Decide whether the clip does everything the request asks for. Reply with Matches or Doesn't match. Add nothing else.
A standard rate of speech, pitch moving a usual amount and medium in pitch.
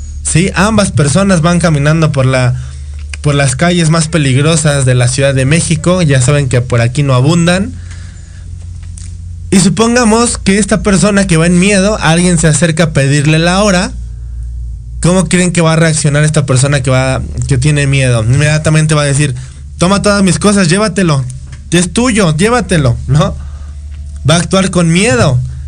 Doesn't match